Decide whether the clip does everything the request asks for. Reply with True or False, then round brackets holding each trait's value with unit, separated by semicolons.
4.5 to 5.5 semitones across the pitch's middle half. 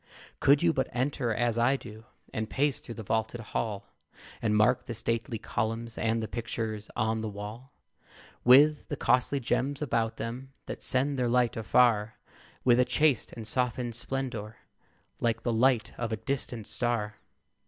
False (2.4 semitones)